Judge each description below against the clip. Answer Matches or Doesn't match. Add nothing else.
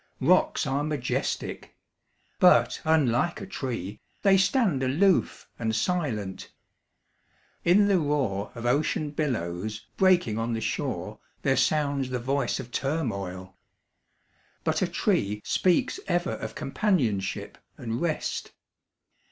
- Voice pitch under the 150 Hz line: Matches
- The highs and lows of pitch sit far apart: Matches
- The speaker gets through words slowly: Matches